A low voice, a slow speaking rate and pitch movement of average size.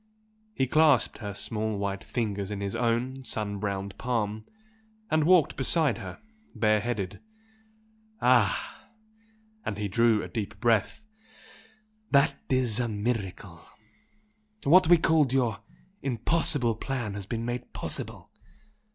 Yes: low, 115 Hz; slow, 125 wpm; average, 4.2 semitones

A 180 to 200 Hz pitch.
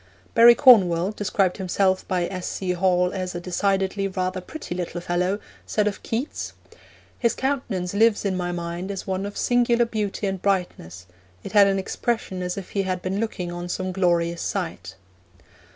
Yes: high, 190 Hz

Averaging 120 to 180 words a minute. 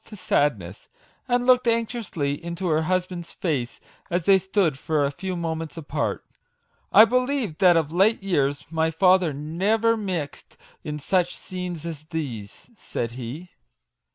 Yes: average, 155 wpm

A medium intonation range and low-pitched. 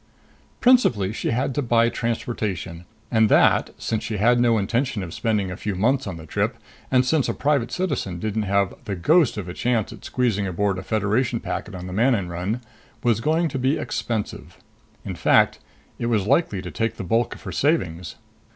Yes: average, 4.2 semitones; low, 110 Hz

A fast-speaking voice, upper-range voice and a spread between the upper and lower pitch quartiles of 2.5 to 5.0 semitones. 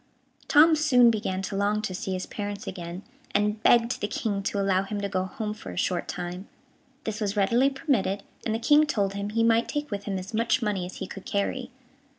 Yes: fast, 220 wpm; high, 205 Hz; average, 3.1 semitones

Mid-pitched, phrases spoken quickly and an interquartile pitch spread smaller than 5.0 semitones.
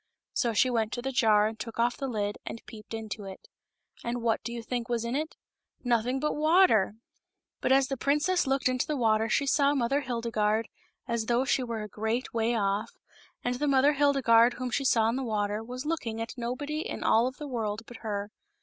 No: high, 235 Hz; fast, 215 wpm; average, 3.3 semitones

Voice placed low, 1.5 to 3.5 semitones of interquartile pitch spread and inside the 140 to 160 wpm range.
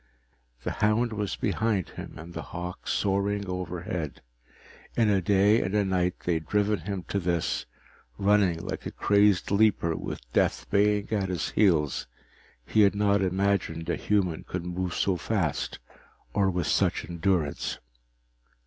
Yes: very low, 95 Hz; average, 2.9 semitones; average, 150 wpm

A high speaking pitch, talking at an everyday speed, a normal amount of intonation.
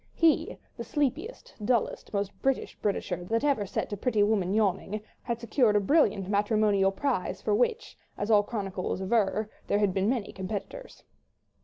Yes: high, 210 Hz; average, 165 wpm; average, 3.7 semitones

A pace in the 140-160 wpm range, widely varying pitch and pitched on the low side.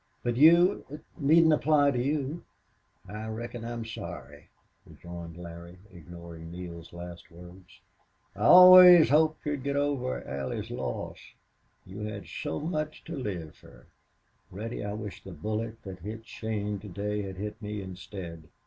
Yes: average, 150 wpm; wide, 8.1 semitones; low, 105 Hz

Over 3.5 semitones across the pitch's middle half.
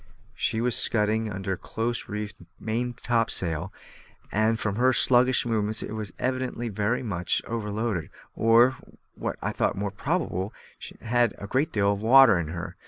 No: average, 3.0 semitones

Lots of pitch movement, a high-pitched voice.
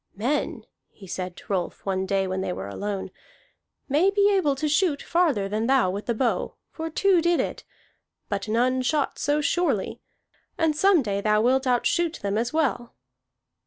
Yes: wide, 7.8 semitones; very high, 255 Hz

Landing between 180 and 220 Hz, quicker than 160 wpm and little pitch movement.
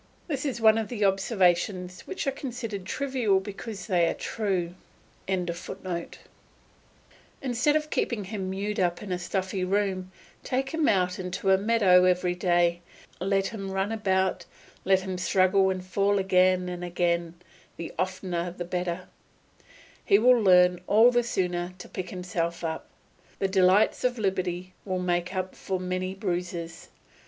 No: medium, 185 Hz; average, 150 wpm; narrow, 2.3 semitones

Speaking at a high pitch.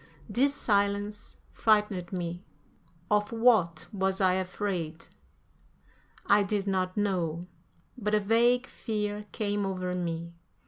Yes: high, 200 Hz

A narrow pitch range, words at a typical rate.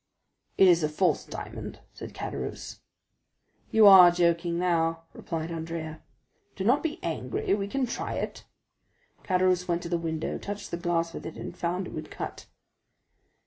Yes: narrow, 2.1 semitones; average, 160 wpm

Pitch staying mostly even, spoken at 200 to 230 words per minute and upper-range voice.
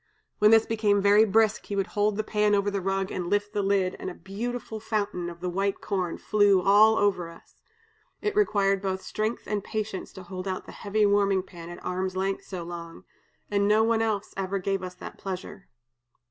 Yes: narrow, 2.0 semitones; fast, 205 wpm; high, 200 Hz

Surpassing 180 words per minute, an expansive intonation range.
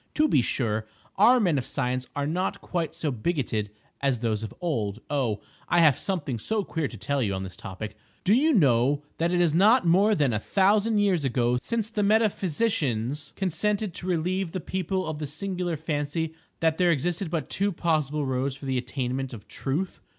Yes: average, 190 wpm; wide, 6.5 semitones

